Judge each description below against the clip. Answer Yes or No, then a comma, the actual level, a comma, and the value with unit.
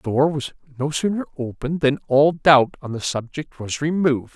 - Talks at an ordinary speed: Yes, average, 195 wpm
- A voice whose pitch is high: No, medium, 140 Hz